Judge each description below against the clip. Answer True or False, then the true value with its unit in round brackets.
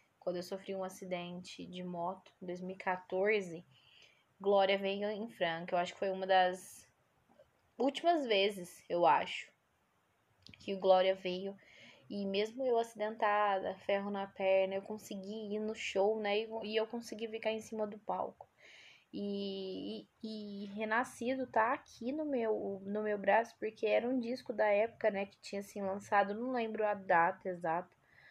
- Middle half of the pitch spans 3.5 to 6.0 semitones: False (2.7 semitones)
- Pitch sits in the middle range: False (200 Hz)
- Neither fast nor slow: True (160 wpm)